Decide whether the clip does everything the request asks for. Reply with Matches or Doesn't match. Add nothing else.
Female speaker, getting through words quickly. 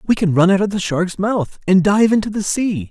Doesn't match